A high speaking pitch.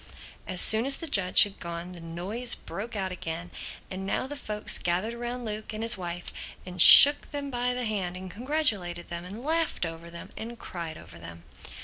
Yes: high, 200 Hz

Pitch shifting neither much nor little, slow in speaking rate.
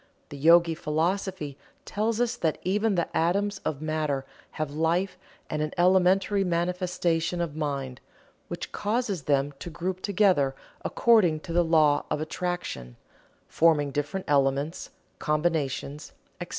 Yes: average, 3.8 semitones; slow, 130 wpm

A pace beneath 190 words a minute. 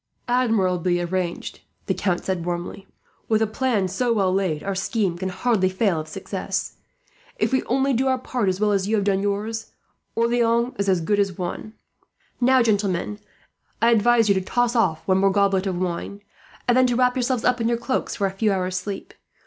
No: average, 200 wpm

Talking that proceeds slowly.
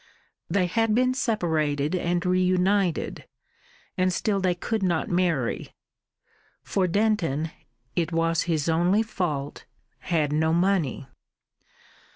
Yes: slow, 110 wpm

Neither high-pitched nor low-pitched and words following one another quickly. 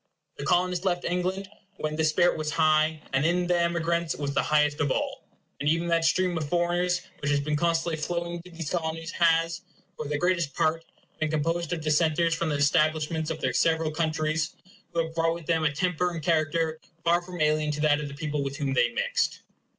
Yes: medium, 160 Hz; fast, 210 wpm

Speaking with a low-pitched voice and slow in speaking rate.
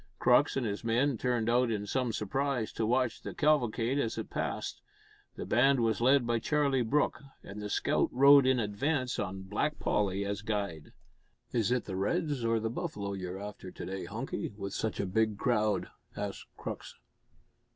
No: low, 115 Hz; average, 180 wpm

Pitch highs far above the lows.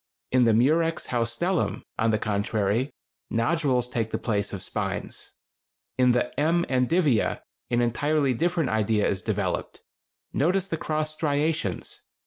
Yes: wide, 5.7 semitones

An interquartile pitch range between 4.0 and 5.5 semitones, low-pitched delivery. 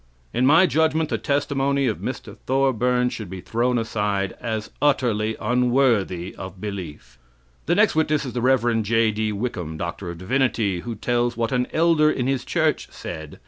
Yes: average, 4.7 semitones; low, 120 Hz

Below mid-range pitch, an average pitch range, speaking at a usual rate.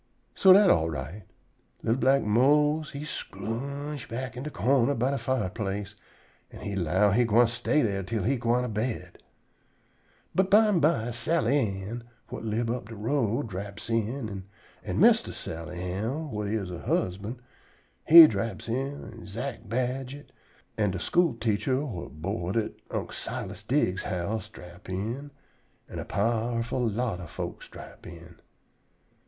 Yes: low, 115 Hz; average, 4.9 semitones; average, 150 wpm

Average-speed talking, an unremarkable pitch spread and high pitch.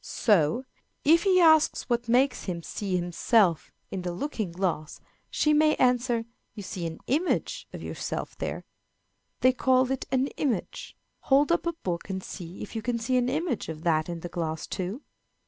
No: average, 180 wpm; wide, 7.2 semitones; high, 230 Hz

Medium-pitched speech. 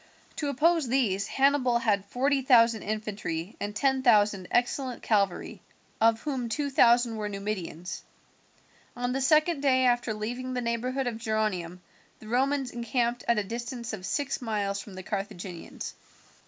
No: high, 235 Hz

